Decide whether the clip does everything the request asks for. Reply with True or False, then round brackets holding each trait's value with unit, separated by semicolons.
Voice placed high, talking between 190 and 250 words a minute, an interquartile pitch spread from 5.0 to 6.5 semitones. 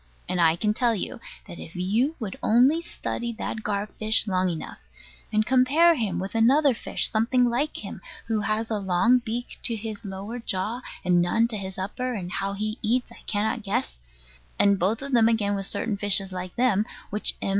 False (215 Hz; 200 wpm; 3.5 semitones)